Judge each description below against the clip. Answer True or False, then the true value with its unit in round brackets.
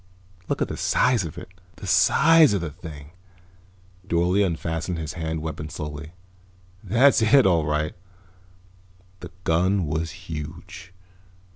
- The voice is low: True (85 Hz)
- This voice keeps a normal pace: False (130 wpm)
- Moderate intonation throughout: True (3.7 semitones)